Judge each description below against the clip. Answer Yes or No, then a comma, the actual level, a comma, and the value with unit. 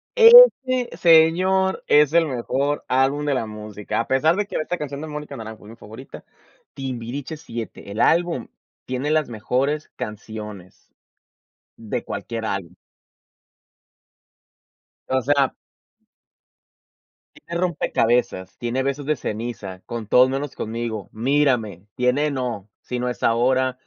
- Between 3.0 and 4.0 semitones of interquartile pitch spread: No, average, 5.0 semitones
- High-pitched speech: No, low, 130 Hz